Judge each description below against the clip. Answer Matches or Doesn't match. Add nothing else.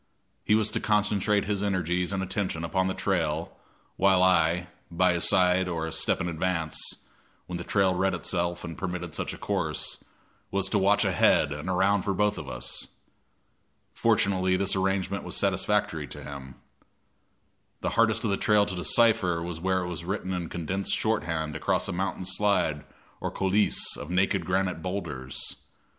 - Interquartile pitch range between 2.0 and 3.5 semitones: Matches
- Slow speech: Doesn't match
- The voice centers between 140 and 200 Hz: Doesn't match